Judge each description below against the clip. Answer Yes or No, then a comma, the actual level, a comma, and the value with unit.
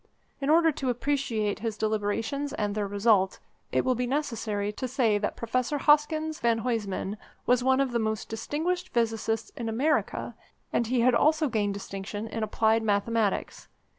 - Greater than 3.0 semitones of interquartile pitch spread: Yes, average, 4.2 semitones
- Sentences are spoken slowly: No, average, 165 wpm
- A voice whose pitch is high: Yes, high, 230 Hz